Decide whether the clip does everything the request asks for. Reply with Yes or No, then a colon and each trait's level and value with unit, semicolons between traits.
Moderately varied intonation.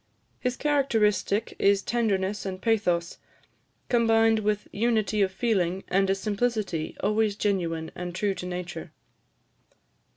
Yes: average, 3.1 semitones